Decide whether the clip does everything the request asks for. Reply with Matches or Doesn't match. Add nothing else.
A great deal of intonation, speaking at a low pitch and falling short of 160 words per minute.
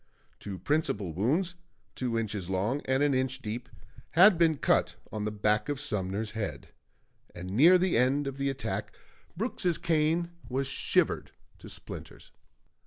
Matches